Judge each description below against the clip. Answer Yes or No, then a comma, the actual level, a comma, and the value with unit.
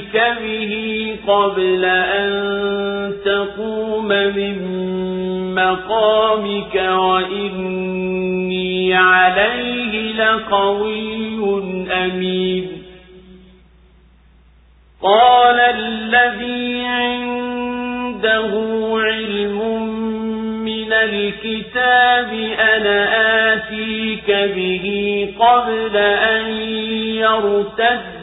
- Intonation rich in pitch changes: No, average, 3.0 semitones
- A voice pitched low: No, high, 215 Hz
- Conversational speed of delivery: No, slow, 45 wpm